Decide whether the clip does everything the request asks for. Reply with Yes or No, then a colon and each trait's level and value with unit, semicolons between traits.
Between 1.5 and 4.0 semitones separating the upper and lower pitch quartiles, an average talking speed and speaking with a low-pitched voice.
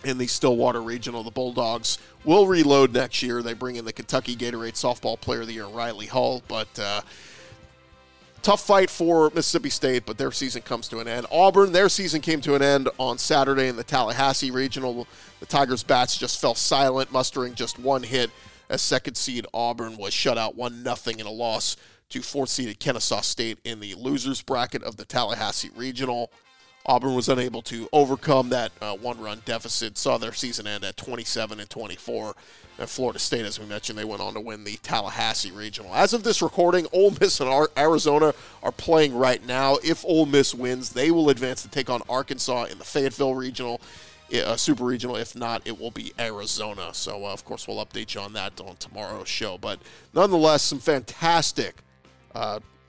Yes: average, 3.3 semitones; average, 190 wpm; low, 125 Hz